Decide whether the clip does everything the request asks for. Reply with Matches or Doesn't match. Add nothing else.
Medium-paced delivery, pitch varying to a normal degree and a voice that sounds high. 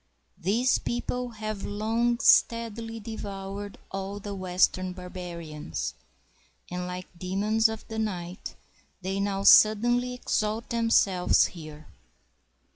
Doesn't match